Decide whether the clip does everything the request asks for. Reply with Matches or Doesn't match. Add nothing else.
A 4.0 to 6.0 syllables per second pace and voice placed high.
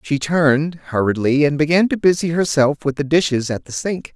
Doesn't match